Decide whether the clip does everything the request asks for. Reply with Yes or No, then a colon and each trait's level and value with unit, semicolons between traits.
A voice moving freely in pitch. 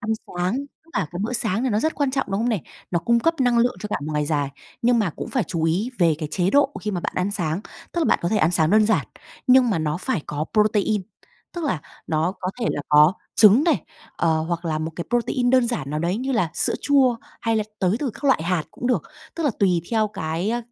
Yes: wide, 6.4 semitones